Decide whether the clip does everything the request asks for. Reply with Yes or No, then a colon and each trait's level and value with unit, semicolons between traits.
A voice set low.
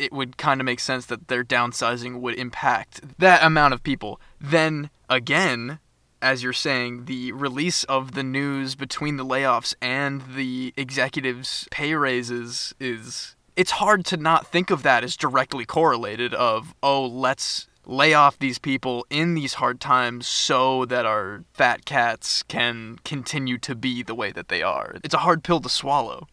Yes: low, 130 Hz